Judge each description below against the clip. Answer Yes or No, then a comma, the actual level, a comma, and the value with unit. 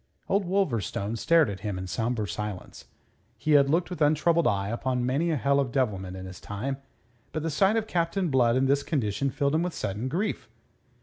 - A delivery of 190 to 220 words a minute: Yes, average, 200 wpm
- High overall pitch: No, low, 135 Hz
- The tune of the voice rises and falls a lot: Yes, wide, 7.4 semitones